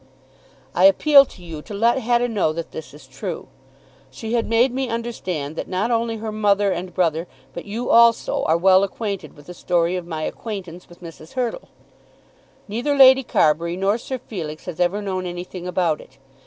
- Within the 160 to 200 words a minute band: Yes, average, 185 wpm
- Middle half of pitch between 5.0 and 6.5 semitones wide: Yes, average, 5.3 semitones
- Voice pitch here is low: No, high, 190 Hz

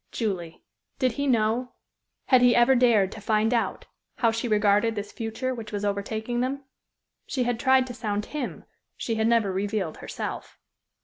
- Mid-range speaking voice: No, high, 225 Hz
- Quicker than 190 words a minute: No, average, 170 wpm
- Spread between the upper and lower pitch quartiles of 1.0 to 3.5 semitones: Yes, average, 3.0 semitones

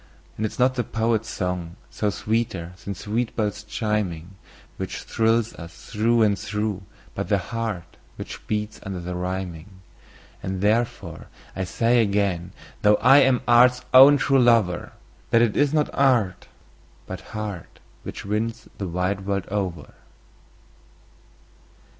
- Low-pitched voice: Yes, low, 105 Hz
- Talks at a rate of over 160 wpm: No, average, 140 wpm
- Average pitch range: Yes, average, 3.8 semitones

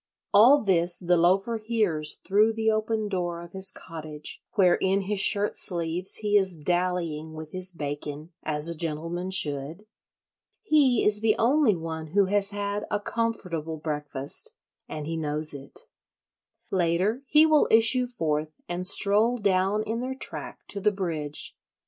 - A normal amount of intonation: Yes, average, 4.8 semitones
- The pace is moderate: Yes, average, 150 wpm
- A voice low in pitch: No, medium, 185 Hz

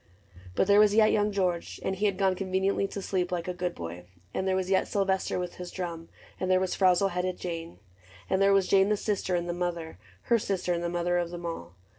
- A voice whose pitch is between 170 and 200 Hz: Yes, medium, 185 Hz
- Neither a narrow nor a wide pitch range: No, narrow, 2.0 semitones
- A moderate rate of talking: No, fast, 260 wpm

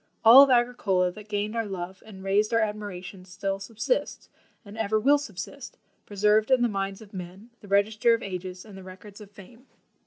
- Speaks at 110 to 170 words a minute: No, average, 190 wpm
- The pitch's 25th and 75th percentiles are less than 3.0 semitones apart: Yes, narrow, 2.6 semitones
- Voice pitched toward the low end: No, high, 205 Hz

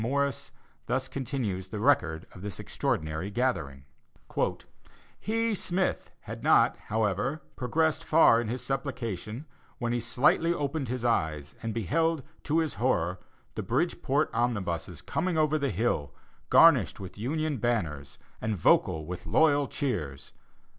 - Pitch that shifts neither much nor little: No, wide, 7.5 semitones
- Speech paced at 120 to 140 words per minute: Yes, slow, 135 wpm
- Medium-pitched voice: No, low, 120 Hz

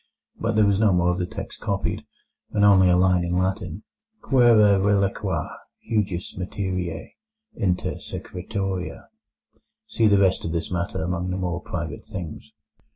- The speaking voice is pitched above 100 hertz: No, very low, 95 Hz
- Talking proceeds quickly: No, average, 145 wpm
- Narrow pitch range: Yes, narrow, 2.3 semitones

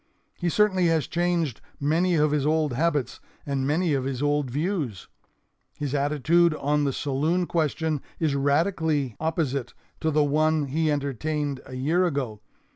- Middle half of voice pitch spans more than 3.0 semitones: No, average, 2.7 semitones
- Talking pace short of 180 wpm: Yes, average, 150 wpm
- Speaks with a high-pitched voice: No, medium, 150 Hz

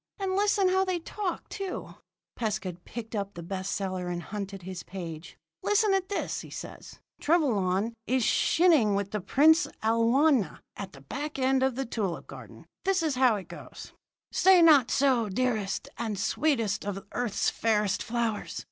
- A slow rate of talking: No, average, 165 wpm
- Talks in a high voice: Yes, high, 230 Hz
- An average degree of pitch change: No, wide, 7.7 semitones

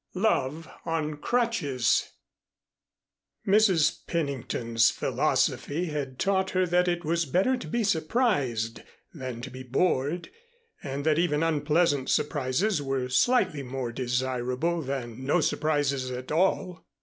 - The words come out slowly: Yes, slow, 125 wpm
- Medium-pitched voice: Yes, medium, 150 Hz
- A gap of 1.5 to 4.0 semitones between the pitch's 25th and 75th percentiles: No, average, 5.3 semitones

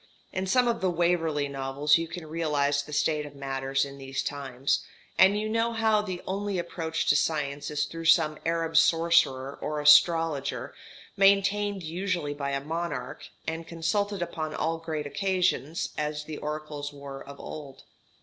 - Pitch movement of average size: Yes, average, 3.5 semitones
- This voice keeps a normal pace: Yes, average, 160 wpm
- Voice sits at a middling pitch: Yes, medium, 160 Hz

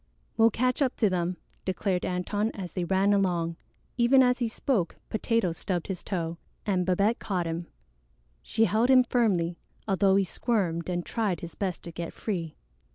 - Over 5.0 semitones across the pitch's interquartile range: No, average, 4.2 semitones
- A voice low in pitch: No, high, 190 Hz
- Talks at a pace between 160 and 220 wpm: Yes, average, 170 wpm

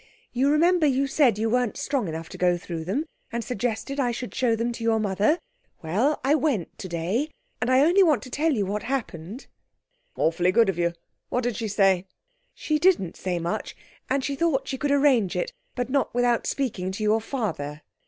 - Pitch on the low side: No, high, 235 Hz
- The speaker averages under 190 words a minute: No, average, 200 wpm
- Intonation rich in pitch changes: Yes, wide, 6.2 semitones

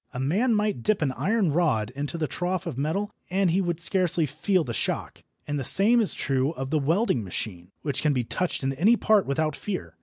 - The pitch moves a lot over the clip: Yes, wide, 6.1 semitones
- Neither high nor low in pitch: Yes, medium, 160 Hz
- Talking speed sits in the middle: No, fast, 220 wpm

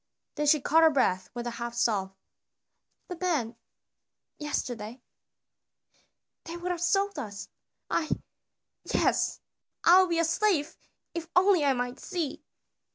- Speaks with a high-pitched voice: Yes, very high, 300 Hz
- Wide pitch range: Yes, wide, 6.4 semitones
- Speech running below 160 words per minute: Yes, slow, 135 wpm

